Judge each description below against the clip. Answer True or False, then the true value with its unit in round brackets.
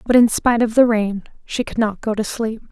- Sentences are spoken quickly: True (265 wpm)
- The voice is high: True (225 Hz)